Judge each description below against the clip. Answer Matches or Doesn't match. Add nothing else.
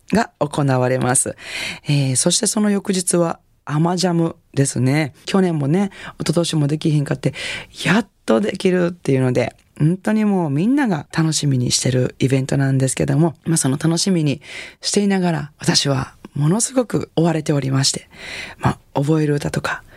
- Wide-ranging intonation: Doesn't match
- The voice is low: Doesn't match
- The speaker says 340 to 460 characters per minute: Matches